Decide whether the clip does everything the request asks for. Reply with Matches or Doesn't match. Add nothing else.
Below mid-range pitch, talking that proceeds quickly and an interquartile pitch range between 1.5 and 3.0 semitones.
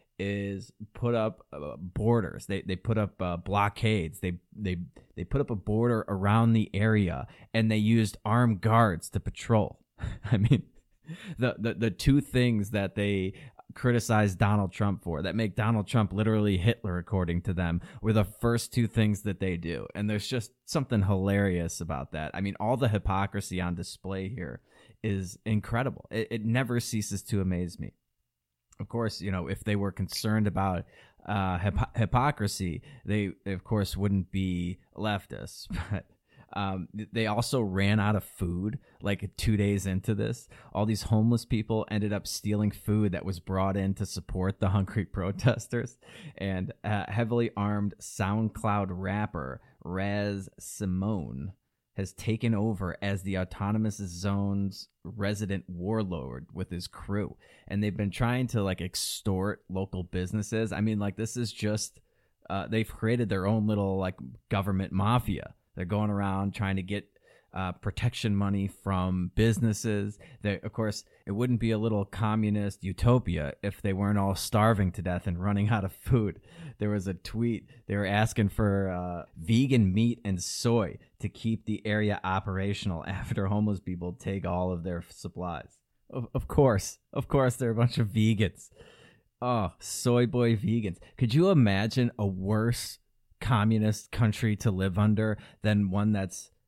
Doesn't match